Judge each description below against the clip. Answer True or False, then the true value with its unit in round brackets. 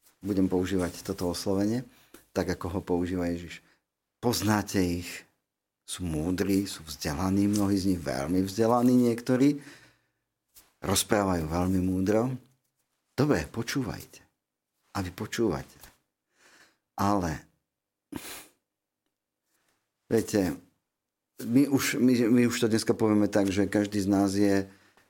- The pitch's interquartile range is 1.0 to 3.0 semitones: False (3.7 semitones)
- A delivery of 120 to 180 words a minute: False (110 wpm)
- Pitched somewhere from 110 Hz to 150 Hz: False (100 Hz)